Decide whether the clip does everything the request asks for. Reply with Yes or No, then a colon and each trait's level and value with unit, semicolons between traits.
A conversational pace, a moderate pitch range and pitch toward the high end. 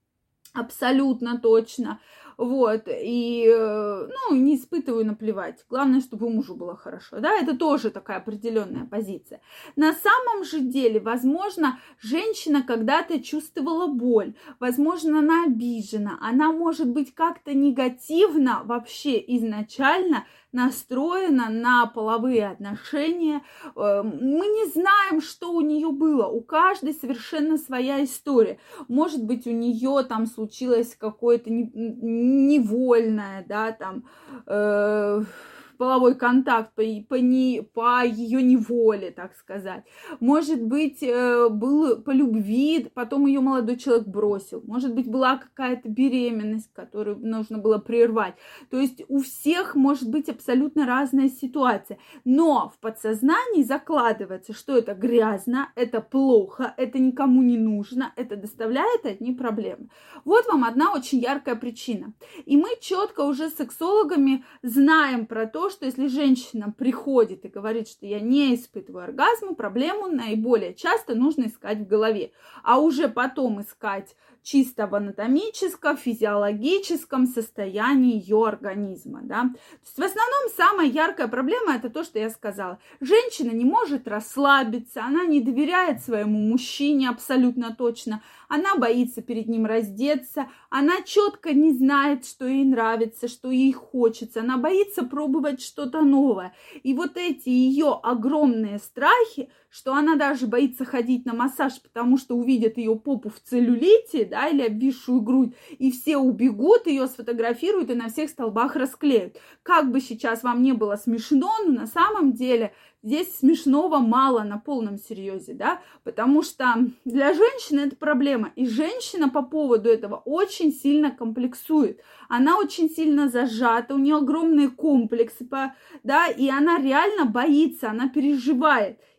Yes: average, 135 wpm; average, 4.3 semitones; very high, 260 Hz